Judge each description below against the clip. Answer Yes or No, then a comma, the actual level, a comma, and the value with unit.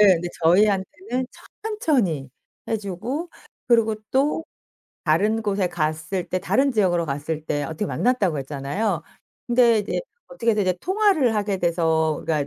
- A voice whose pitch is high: Yes, high, 200 Hz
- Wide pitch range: Yes, wide, 6.7 semitones